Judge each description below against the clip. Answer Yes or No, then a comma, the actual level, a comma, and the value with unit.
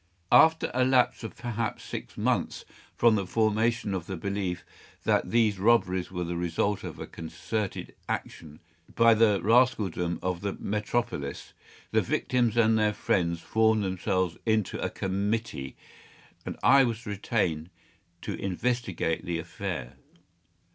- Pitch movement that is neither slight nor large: Yes, average, 4.4 semitones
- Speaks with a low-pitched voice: Yes, low, 105 Hz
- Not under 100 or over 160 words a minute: Yes, slow, 135 wpm